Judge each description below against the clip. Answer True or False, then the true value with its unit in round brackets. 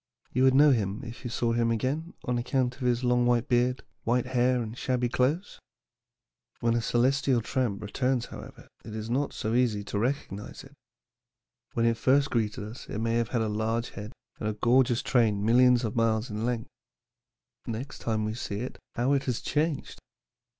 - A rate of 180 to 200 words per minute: True (190 wpm)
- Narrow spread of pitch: True (2.3 semitones)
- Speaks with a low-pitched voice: True (120 Hz)